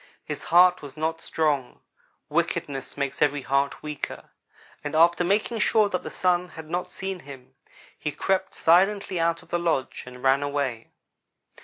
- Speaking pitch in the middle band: Yes, medium, 160 Hz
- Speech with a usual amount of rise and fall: Yes, average, 4.3 semitones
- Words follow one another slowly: No, average, 160 wpm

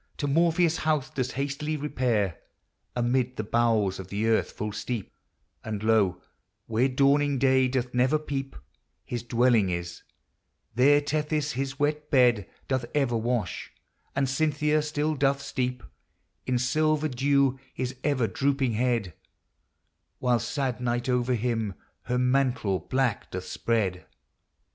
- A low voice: Yes, low, 125 Hz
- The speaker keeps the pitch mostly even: No, average, 3.4 semitones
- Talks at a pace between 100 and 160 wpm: Yes, slow, 135 wpm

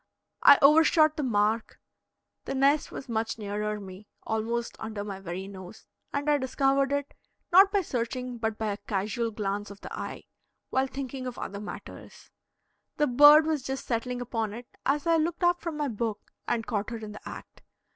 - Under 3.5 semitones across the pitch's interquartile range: No, average, 5.1 semitones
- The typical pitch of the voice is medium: No, high, 240 Hz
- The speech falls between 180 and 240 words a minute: Yes, average, 185 wpm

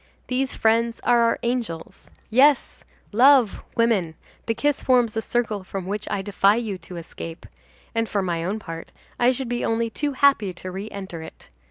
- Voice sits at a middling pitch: No, high, 225 Hz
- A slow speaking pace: No, average, 180 wpm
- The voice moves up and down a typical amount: Yes, average, 4.1 semitones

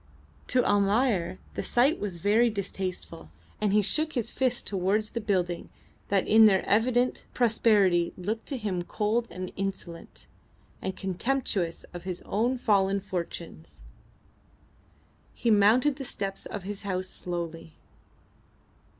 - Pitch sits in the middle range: No, high, 200 Hz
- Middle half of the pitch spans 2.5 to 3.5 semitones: No, average, 3.9 semitones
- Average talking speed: No, slow, 130 wpm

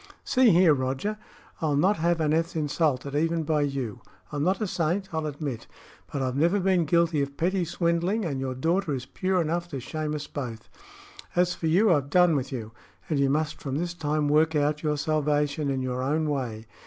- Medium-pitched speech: Yes, medium, 155 Hz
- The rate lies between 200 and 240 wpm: Yes, fast, 205 wpm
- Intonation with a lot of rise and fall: No, average, 3.4 semitones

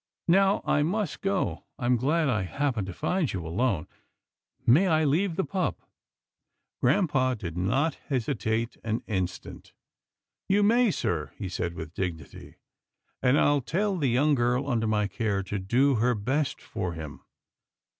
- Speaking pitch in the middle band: No, low, 125 Hz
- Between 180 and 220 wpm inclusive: No, average, 165 wpm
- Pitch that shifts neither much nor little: No, wide, 7.6 semitones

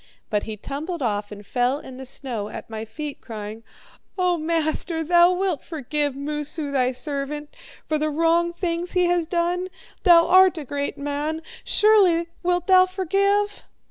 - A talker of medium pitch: No, very high, 315 Hz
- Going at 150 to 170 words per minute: Yes, average, 160 wpm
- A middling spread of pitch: Yes, average, 4.3 semitones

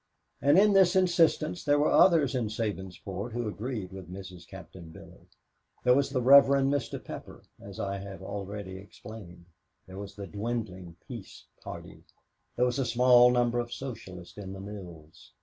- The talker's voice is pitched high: No, low, 110 Hz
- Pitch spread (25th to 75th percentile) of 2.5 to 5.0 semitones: No, wide, 5.4 semitones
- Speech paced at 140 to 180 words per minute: Yes, average, 165 wpm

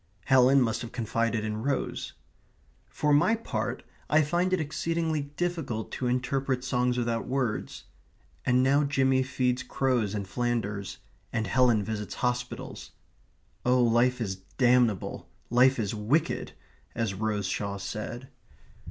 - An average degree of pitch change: Yes, average, 3.3 semitones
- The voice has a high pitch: No, low, 125 Hz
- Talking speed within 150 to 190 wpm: No, slow, 135 wpm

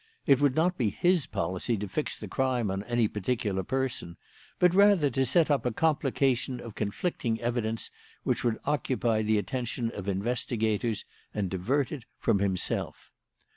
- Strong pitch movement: No, average, 4.4 semitones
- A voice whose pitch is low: Yes, low, 120 Hz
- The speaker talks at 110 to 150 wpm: No, average, 160 wpm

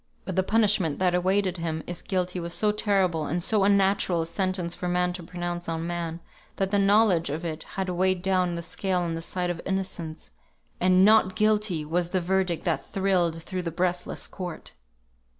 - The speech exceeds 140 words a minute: Yes, average, 190 wpm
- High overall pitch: No, medium, 180 Hz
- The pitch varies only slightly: Yes, narrow, 2.1 semitones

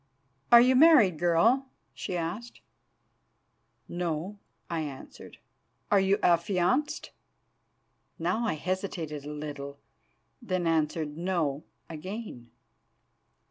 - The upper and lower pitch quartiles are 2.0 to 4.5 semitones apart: No, average, 4.9 semitones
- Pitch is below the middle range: No, medium, 175 Hz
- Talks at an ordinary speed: No, slow, 95 wpm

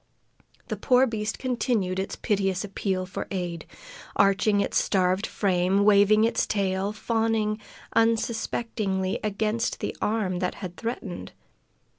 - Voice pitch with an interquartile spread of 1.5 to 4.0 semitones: Yes, average, 2.8 semitones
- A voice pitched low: No, high, 205 Hz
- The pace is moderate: No, slow, 120 wpm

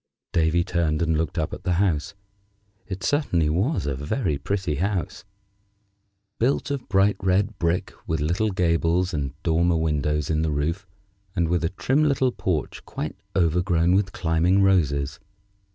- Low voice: Yes, very low, 85 Hz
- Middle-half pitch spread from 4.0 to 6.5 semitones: No, average, 3.6 semitones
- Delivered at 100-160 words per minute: Yes, average, 150 wpm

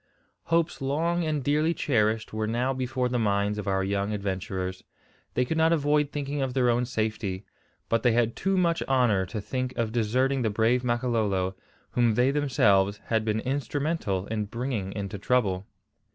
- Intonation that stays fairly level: No, average, 4.6 semitones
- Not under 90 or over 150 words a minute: No, average, 170 wpm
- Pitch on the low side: Yes, low, 120 Hz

